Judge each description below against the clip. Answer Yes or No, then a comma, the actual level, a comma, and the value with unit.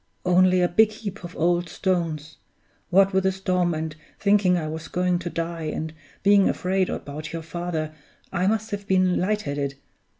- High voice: No, medium, 180 Hz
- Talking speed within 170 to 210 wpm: Yes, average, 175 wpm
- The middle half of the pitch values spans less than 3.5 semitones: Yes, average, 2.8 semitones